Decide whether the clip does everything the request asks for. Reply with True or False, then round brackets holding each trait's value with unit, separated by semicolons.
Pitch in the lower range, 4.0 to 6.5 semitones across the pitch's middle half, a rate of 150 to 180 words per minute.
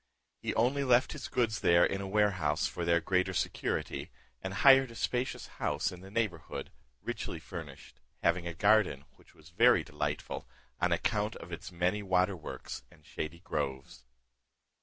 True (95 Hz; 4.3 semitones; 160 wpm)